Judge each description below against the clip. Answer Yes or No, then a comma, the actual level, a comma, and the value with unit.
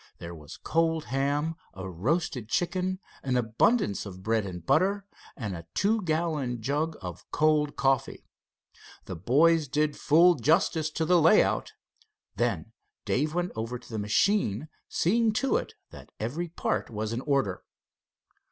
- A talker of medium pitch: Yes, medium, 145 Hz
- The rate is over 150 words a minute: No, average, 145 wpm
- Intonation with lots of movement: Yes, wide, 7.0 semitones